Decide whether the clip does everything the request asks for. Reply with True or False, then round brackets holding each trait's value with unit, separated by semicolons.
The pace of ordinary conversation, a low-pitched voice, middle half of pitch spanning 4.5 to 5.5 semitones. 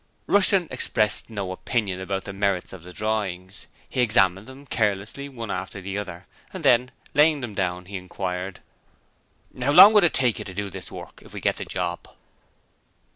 True (180 wpm; 100 Hz; 5.1 semitones)